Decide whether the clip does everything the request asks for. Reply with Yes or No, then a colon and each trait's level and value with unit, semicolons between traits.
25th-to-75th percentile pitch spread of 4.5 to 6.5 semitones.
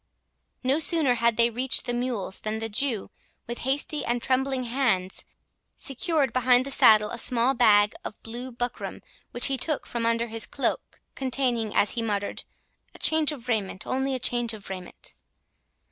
No: average, 2.9 semitones